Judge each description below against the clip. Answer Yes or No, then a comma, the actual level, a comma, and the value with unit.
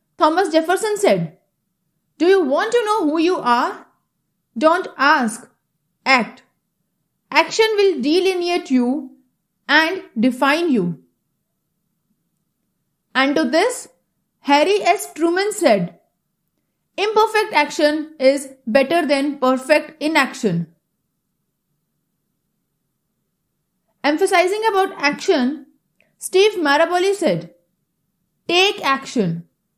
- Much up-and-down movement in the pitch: Yes, wide, 8.7 semitones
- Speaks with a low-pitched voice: No, very high, 285 Hz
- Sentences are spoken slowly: Yes, slow, 85 wpm